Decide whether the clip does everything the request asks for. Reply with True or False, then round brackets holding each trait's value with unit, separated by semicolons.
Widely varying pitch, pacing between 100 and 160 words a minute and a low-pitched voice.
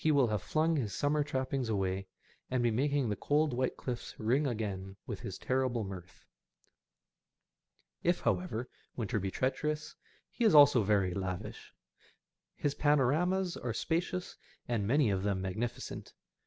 True (6.2 semitones; 140 wpm; 125 Hz)